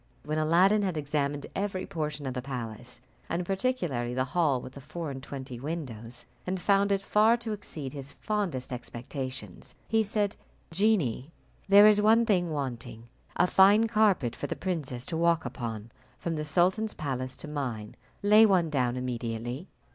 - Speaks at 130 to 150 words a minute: No, average, 165 wpm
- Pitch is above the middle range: No, medium, 155 Hz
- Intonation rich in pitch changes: Yes, wide, 7.2 semitones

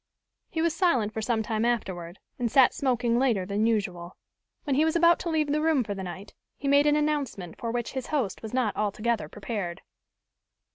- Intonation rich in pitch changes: Yes, wide, 5.8 semitones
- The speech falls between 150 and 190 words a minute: No, average, 200 wpm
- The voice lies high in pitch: Yes, high, 235 Hz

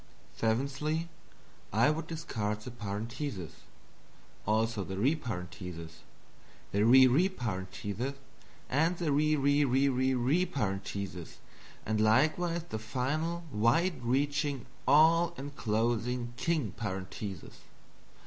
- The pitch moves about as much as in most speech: No, wide, 5.9 semitones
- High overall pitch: No, low, 125 Hz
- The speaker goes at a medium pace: No, slow, 100 wpm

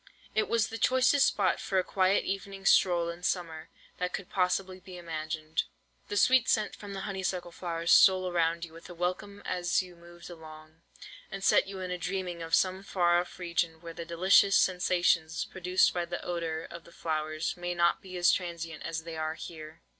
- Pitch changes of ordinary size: No, narrow, 2.1 semitones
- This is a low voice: No, medium, 175 Hz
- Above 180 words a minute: Yes, average, 190 wpm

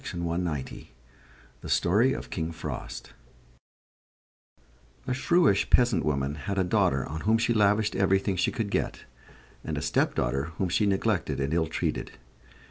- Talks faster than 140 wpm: No, slow, 135 wpm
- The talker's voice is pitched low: Yes, very low, 95 Hz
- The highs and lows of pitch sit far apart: Yes, wide, 5.7 semitones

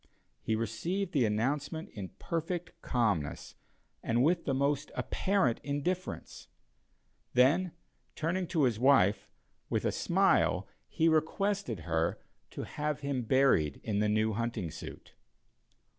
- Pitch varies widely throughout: Yes, wide, 6.8 semitones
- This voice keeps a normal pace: No, slow, 125 wpm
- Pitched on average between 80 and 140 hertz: Yes, low, 135 Hz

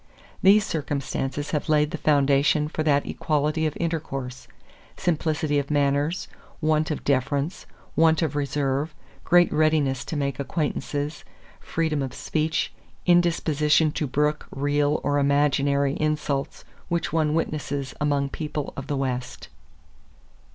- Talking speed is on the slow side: Yes, slow, 125 wpm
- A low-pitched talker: No, medium, 150 Hz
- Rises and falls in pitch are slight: Yes, narrow, 1.9 semitones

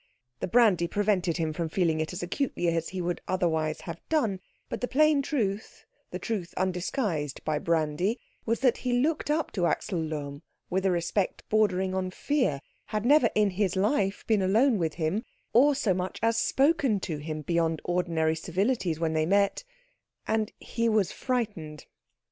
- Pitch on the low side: No, high, 190 Hz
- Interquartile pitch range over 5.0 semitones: Yes, wide, 5.4 semitones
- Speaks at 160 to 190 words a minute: Yes, average, 170 wpm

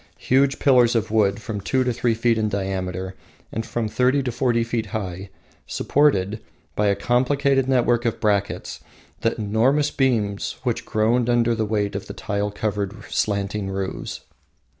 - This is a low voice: Yes, low, 110 Hz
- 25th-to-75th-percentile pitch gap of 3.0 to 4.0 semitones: Yes, average, 3.3 semitones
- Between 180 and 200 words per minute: No, average, 155 wpm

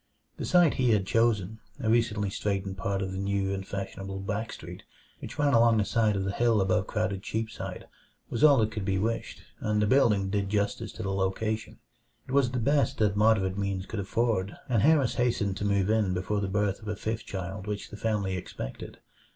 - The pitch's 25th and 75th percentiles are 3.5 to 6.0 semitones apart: No, average, 2.7 semitones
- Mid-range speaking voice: No, low, 105 Hz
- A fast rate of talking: Yes, fast, 210 wpm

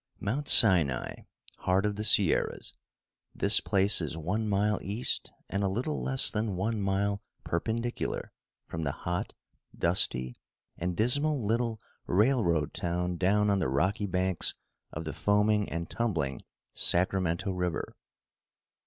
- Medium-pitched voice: No, low, 100 Hz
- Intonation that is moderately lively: Yes, average, 3.7 semitones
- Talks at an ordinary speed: No, slow, 130 wpm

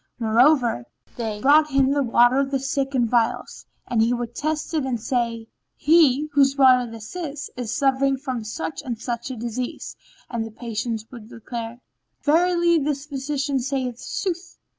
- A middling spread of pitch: Yes, average, 3.3 semitones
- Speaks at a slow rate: No, average, 165 wpm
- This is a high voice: Yes, very high, 260 Hz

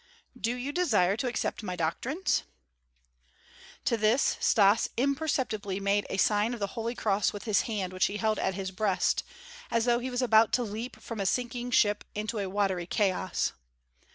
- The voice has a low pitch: No, high, 215 Hz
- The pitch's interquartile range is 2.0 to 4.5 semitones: Yes, average, 3.4 semitones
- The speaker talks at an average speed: Yes, average, 180 wpm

